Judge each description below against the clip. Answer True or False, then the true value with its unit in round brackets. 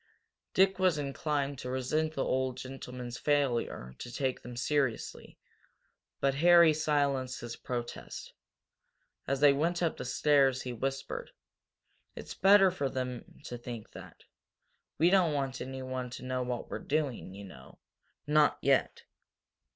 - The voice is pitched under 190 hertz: True (135 Hz)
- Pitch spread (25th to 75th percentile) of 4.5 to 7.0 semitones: False (3.0 semitones)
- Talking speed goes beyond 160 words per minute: False (140 wpm)